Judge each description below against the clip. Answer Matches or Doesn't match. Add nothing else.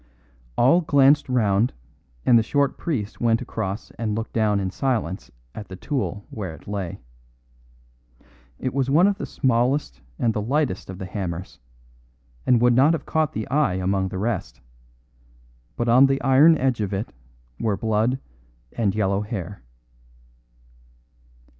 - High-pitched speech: Doesn't match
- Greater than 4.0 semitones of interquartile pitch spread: Matches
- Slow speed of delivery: Doesn't match